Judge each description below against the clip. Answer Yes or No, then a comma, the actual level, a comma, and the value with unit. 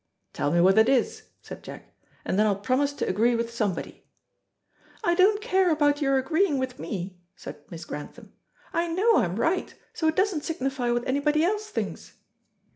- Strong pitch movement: Yes, wide, 7.5 semitones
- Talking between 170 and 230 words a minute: Yes, average, 180 wpm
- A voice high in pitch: Yes, very high, 270 Hz